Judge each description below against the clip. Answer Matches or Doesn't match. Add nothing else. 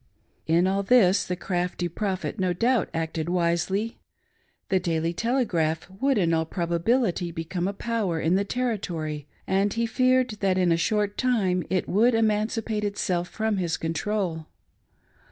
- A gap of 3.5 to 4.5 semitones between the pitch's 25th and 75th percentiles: Matches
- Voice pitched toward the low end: Doesn't match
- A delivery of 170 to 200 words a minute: Doesn't match